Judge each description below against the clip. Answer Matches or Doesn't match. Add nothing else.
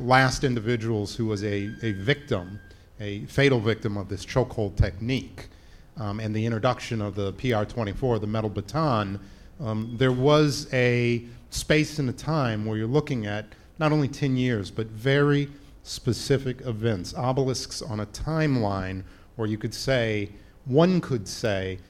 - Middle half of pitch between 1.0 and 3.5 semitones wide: Doesn't match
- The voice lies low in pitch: Matches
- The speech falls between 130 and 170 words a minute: Matches